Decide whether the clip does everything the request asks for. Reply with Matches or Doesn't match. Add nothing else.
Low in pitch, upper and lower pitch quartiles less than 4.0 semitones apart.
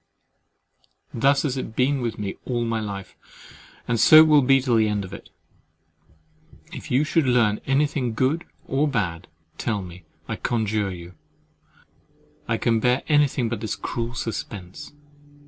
Doesn't match